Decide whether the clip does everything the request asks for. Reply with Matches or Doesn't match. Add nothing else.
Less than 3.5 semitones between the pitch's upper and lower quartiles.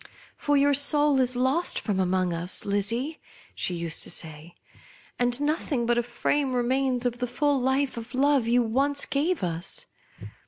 Doesn't match